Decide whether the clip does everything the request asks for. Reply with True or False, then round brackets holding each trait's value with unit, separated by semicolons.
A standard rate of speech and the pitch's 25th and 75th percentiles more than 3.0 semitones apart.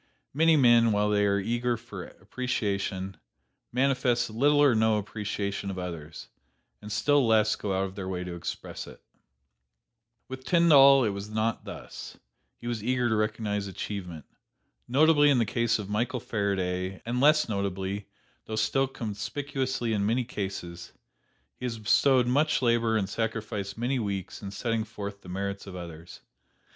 True (155 wpm; 3.9 semitones)